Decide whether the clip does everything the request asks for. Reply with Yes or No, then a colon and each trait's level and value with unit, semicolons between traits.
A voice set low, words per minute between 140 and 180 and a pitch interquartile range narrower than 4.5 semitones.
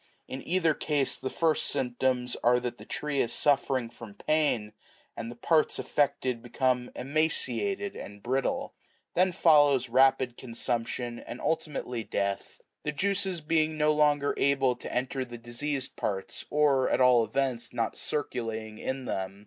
Yes: low, 130 Hz; average, 150 wpm; average, 3.8 semitones